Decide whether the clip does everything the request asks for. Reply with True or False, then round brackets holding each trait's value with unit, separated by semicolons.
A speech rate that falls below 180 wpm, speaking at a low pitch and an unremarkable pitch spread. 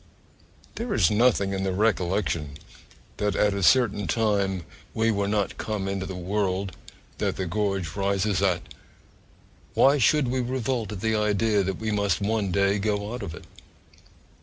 False (160 wpm; 100 Hz; 2.3 semitones)